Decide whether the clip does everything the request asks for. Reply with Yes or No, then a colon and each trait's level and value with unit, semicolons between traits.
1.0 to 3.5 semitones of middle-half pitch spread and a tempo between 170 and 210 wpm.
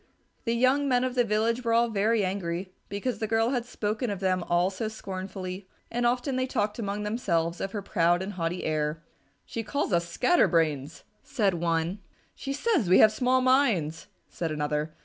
No: wide, 5.4 semitones; average, 190 wpm